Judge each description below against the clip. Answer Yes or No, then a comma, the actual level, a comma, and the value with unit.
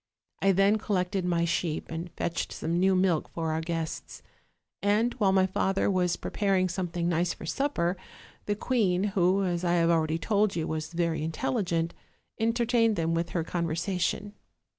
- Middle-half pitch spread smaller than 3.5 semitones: Yes, average, 2.9 semitones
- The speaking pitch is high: No, medium, 180 Hz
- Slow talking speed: No, average, 160 wpm